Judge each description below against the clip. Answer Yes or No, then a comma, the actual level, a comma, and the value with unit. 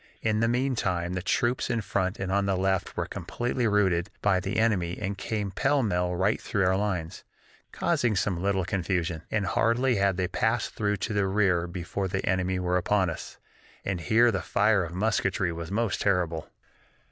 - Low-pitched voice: Yes, very low, 95 Hz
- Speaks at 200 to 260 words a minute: No, average, 185 wpm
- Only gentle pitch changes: No, average, 3.0 semitones